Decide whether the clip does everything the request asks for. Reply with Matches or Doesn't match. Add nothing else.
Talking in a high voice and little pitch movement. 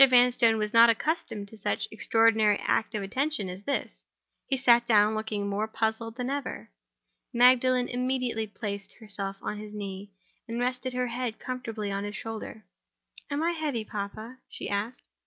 Doesn't match